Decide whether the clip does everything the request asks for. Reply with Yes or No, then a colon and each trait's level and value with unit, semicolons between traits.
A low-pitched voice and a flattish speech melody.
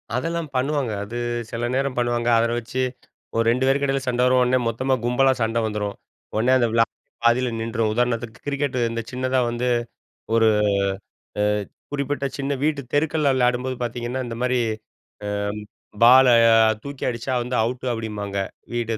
Yes: low, 125 Hz; narrow, 2.3 semitones